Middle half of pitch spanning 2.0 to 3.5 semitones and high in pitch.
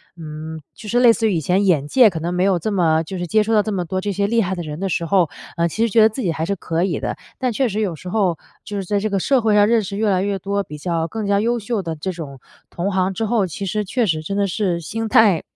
No: average, 4.0 semitones; high, 195 Hz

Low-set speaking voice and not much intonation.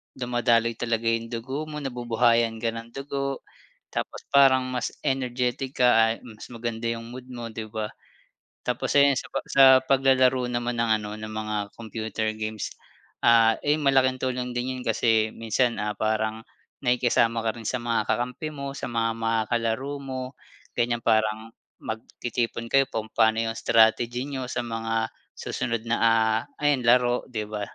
Yes: low, 120 Hz; narrow, 2.2 semitones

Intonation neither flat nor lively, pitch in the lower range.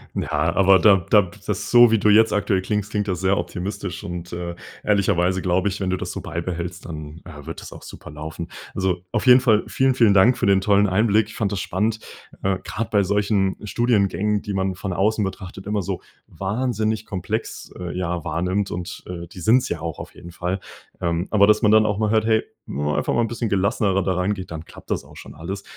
Yes: average, 3.0 semitones; very low, 95 Hz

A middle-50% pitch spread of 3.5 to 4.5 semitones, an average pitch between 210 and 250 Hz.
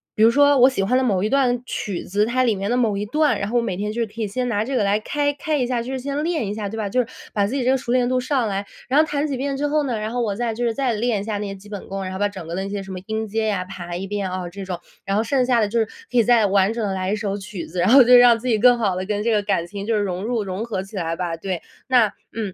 Yes: average, 3.9 semitones; high, 220 Hz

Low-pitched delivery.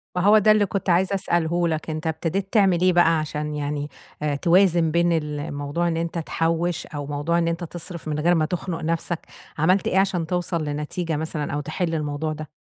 No: medium, 165 Hz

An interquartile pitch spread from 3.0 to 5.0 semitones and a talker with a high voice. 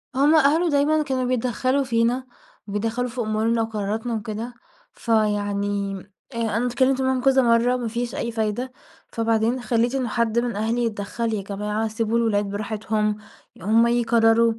No: narrow, 2.5 semitones; high, 230 Hz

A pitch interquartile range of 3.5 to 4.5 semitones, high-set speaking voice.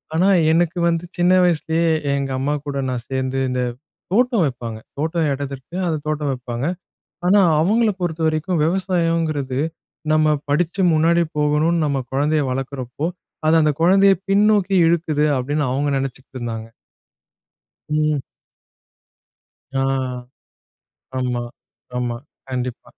No: average, 4.1 semitones; medium, 155 Hz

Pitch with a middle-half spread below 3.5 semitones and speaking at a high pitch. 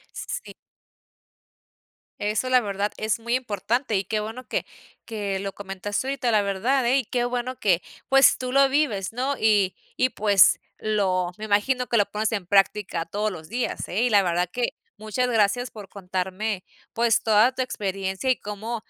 No: average, 3.8 semitones; high, 215 Hz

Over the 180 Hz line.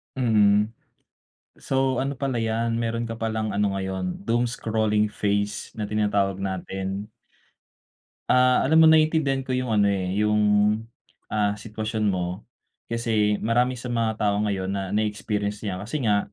No: low, 105 Hz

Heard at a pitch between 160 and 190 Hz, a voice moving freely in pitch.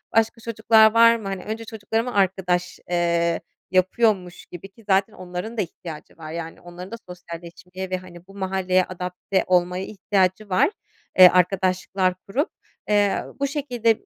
No: medium, 185 Hz; average, 3.4 semitones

